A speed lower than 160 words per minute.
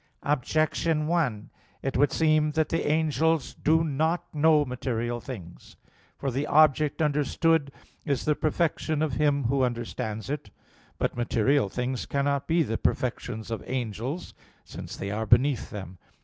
Yes: average, 145 wpm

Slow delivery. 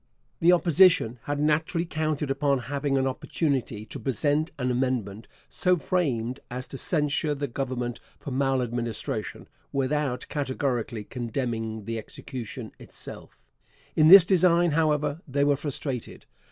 Yes: slow, 125 wpm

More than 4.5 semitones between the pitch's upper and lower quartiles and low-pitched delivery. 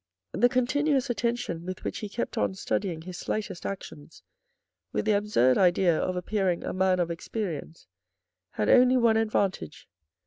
No: average, 5.0 semitones; high, 195 Hz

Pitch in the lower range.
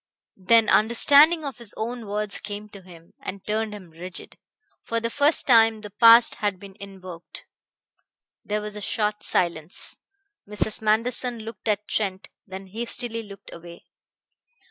No: high, 210 Hz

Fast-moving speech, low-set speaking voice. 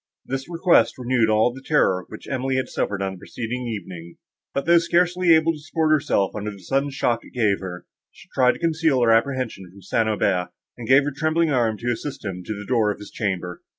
Yes: fast, 220 wpm; low, 120 Hz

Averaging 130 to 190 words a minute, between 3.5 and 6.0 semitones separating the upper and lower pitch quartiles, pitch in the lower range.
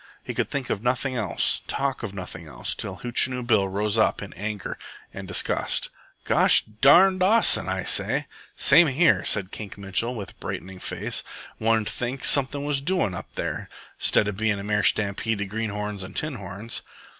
Yes: average, 180 wpm; average, 4.8 semitones; low, 110 Hz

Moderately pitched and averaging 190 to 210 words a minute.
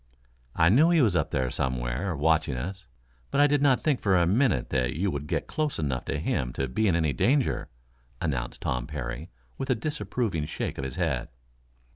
No: very low, 80 Hz; average, 200 wpm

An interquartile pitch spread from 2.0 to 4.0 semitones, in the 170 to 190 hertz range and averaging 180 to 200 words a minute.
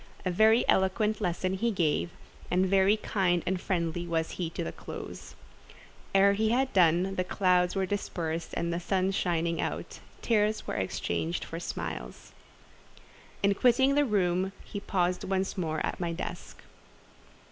No: average, 2.8 semitones; medium, 185 Hz; average, 150 wpm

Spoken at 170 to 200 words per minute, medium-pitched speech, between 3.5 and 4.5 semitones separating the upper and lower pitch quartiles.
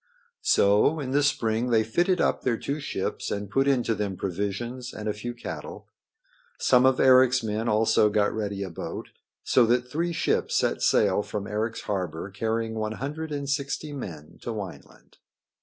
No: average, 175 wpm; low, 115 Hz; average, 4.1 semitones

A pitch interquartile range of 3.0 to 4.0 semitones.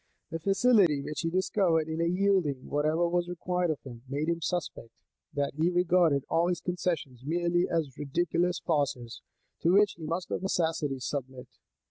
Yes: average, 3.4 semitones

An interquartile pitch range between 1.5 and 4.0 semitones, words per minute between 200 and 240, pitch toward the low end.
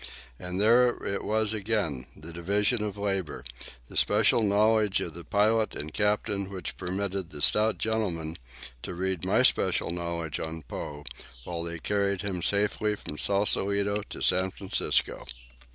No: average, 3.4 semitones; average, 150 wpm; low, 100 Hz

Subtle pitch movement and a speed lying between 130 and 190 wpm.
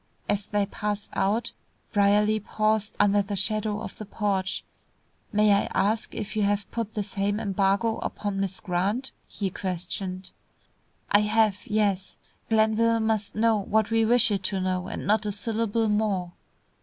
Yes: narrow, 1.7 semitones; average, 155 wpm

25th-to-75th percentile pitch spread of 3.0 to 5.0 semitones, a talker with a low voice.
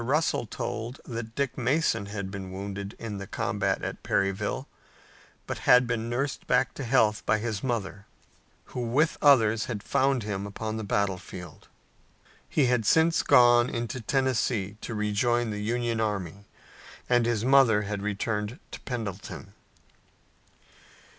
Yes: average, 3.3 semitones; low, 115 Hz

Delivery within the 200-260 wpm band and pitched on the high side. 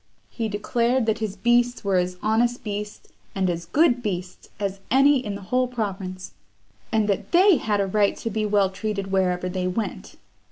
No: average, 185 wpm; high, 210 Hz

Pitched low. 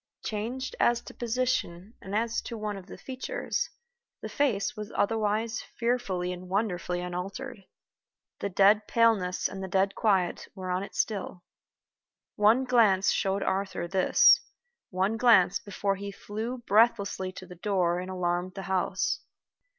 No: high, 200 Hz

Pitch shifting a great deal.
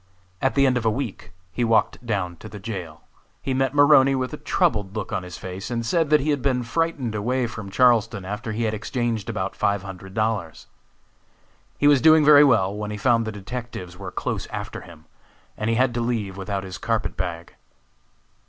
No: average, 4.7 semitones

